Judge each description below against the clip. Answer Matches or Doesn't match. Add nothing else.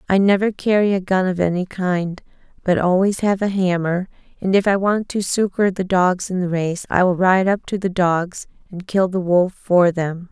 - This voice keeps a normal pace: Doesn't match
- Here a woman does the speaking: Matches